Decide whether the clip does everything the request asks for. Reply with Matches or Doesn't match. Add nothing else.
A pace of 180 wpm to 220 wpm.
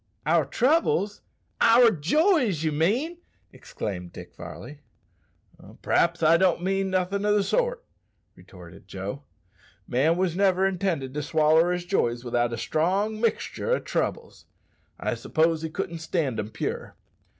Doesn't match